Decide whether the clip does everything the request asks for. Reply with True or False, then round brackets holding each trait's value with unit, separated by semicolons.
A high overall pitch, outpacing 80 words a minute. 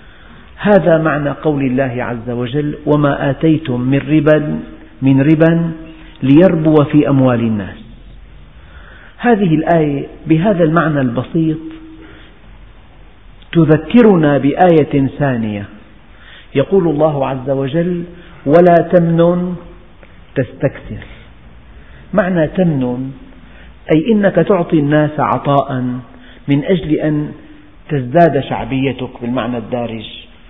False (140 Hz; 90 wpm)